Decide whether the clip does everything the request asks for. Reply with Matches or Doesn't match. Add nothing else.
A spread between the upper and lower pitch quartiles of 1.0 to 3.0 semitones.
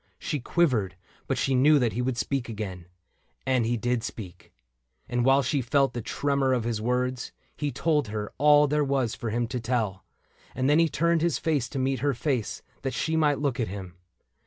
Doesn't match